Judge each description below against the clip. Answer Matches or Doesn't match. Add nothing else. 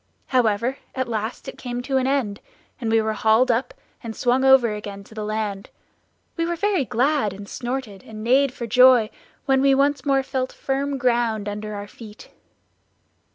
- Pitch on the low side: Doesn't match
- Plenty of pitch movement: Doesn't match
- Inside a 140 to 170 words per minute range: Doesn't match